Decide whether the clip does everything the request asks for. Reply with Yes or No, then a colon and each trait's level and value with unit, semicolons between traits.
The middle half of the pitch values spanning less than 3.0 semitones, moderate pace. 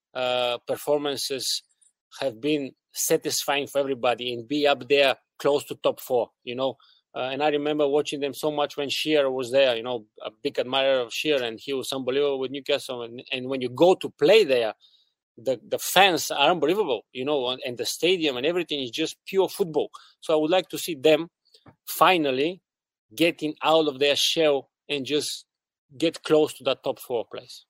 Yes: narrow, 2.6 semitones; average, 195 wpm